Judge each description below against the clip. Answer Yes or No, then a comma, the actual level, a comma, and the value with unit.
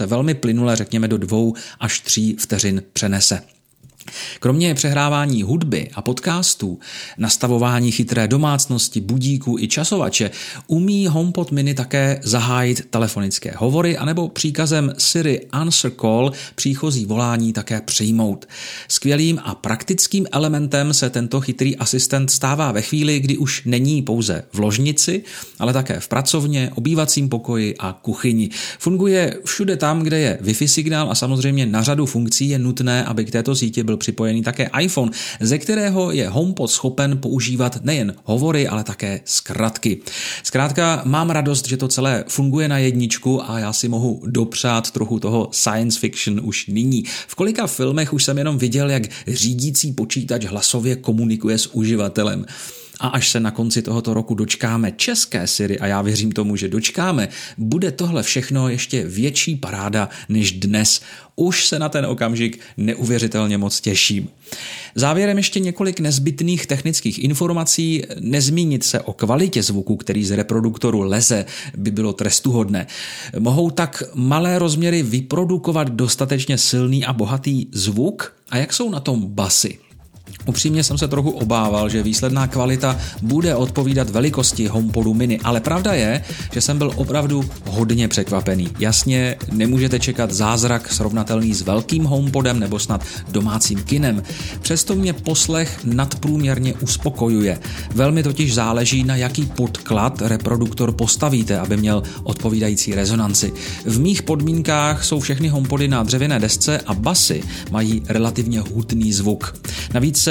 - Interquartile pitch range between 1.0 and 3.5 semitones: No, average, 4.5 semitones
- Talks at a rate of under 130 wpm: No, average, 145 wpm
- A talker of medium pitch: No, low, 125 Hz